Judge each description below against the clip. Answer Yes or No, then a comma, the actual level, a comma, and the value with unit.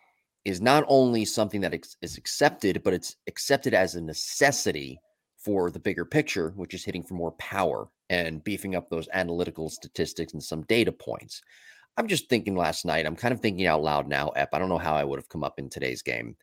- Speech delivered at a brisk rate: Yes, fast, 210 wpm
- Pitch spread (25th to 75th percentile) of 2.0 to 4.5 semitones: No, average, 5.2 semitones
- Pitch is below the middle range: Yes, very low, 90 Hz